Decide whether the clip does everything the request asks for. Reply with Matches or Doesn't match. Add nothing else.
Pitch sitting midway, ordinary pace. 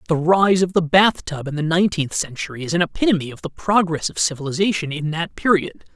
Doesn't match